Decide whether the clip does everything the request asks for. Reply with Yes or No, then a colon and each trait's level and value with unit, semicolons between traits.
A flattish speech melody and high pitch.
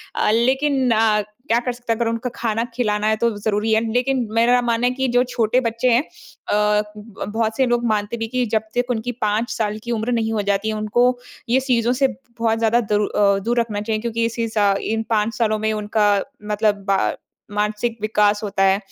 Yes: narrow, 2.3 semitones; high, 225 Hz